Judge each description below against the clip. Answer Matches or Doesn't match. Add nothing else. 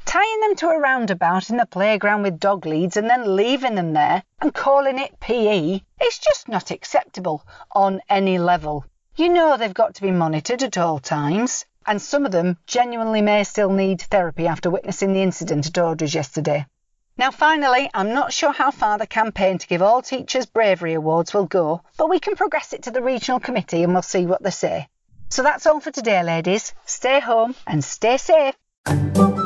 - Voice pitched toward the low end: Doesn't match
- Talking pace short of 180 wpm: Doesn't match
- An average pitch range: Doesn't match